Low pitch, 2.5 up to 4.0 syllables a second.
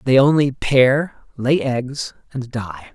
Yes: low, 130 Hz; 3.2 syllables/s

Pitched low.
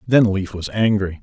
Yes: low, 100 Hz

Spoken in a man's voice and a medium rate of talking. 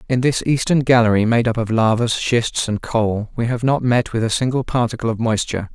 No: male; fast, 220 wpm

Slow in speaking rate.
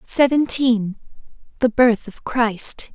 Yes: slow, 100 wpm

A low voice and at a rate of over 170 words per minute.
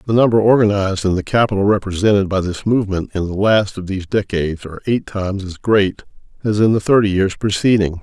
Yes: low, 100 Hz; average, 200 wpm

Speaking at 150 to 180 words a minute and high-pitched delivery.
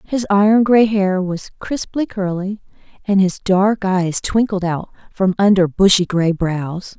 Yes: average, 155 wpm; high, 195 Hz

